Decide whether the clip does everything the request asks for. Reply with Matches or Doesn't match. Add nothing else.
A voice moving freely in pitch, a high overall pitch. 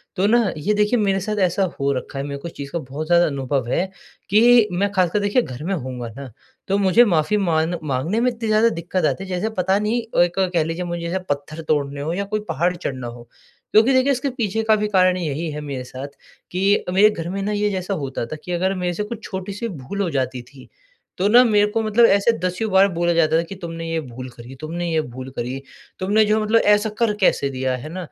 Doesn't match